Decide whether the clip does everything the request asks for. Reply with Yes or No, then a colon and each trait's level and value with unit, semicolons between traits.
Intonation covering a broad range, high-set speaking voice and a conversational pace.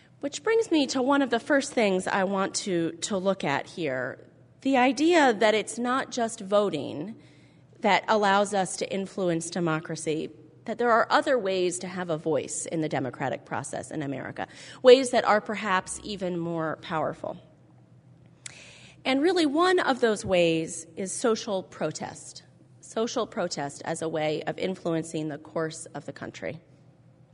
Yes: wide, 6.6 semitones; high, 195 Hz; average, 160 wpm